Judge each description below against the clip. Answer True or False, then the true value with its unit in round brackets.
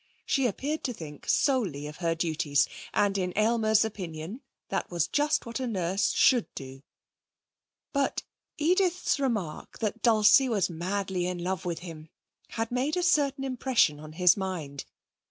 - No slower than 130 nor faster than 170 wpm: True (155 wpm)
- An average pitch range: False (7.2 semitones)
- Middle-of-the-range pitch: False (200 Hz)